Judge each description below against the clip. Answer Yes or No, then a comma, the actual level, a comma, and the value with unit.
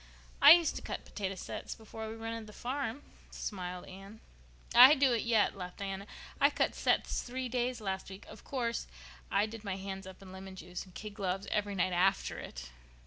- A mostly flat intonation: No, average, 3.2 semitones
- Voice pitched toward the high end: Yes, high, 205 Hz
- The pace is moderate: No, fast, 210 wpm